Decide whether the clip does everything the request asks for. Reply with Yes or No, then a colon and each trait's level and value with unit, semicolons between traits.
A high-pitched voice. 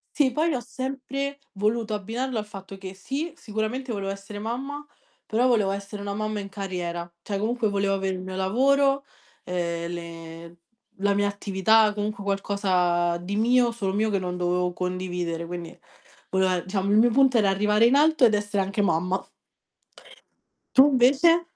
Yes: high, 205 Hz